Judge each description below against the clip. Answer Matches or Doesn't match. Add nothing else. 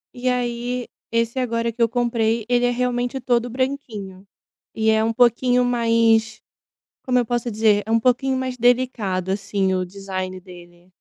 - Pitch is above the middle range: Matches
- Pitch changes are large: Doesn't match